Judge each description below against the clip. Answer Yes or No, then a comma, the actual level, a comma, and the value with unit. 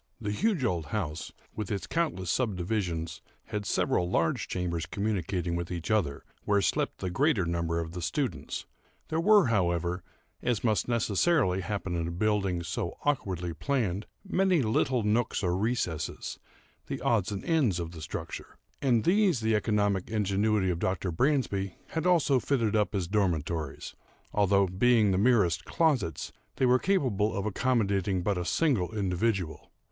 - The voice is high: No, low, 100 Hz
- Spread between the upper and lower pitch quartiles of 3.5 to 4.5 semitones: No, average, 5.2 semitones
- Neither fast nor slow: Yes, average, 155 wpm